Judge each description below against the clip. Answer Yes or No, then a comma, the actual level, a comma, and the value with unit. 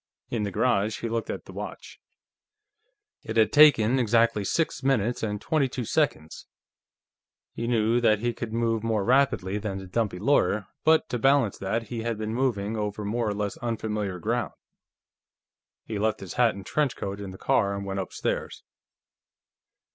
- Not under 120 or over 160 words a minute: No, average, 170 wpm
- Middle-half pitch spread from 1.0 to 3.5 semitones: Yes, average, 3.0 semitones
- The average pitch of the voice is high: No, low, 110 Hz